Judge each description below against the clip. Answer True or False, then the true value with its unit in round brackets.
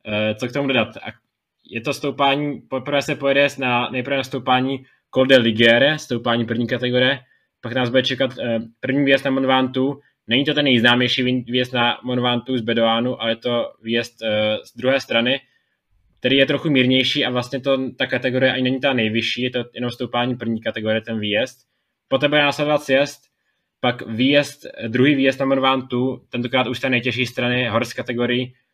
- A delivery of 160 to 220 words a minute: True (170 wpm)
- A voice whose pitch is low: True (125 Hz)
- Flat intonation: True (2.0 semitones)